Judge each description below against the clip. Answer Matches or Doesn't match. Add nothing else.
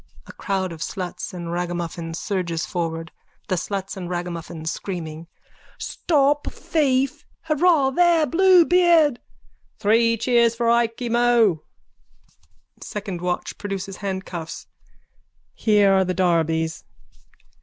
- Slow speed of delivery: Matches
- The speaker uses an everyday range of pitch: Doesn't match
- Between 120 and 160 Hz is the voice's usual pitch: Doesn't match